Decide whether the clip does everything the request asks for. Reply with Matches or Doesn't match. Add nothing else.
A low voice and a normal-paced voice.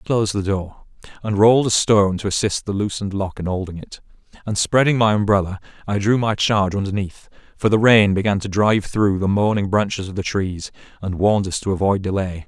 Doesn't match